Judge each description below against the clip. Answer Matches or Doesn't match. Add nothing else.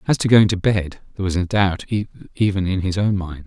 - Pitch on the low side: Matches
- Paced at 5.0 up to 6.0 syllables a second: Matches